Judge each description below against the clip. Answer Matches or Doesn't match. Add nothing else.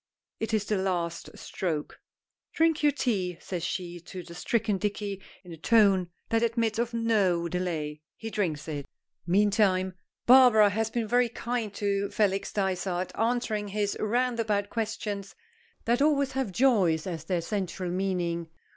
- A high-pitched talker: Matches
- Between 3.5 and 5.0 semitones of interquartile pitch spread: Matches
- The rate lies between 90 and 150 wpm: Matches